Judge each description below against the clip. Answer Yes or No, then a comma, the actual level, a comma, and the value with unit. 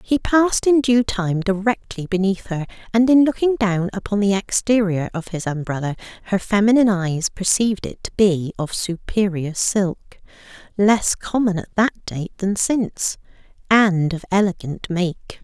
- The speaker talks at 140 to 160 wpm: Yes, average, 145 wpm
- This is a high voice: Yes, high, 200 Hz